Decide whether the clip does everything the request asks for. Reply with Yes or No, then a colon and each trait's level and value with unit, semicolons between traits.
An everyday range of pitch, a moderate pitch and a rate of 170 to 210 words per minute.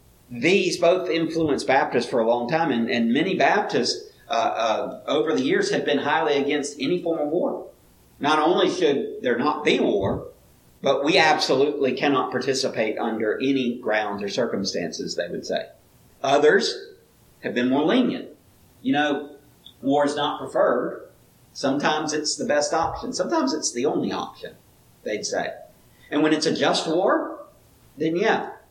No: average, 4.0 semitones; medium, 155 Hz; average, 160 wpm